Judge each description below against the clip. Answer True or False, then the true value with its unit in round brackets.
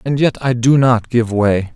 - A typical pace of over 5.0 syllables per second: False (4.2 syllables/s)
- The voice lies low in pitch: True (120 Hz)